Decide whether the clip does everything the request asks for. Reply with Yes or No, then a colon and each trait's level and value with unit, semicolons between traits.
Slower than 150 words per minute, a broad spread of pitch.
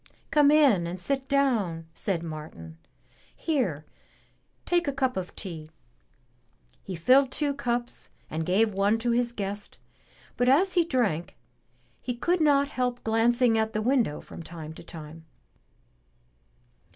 Yes: average, 140 wpm; wide, 7.9 semitones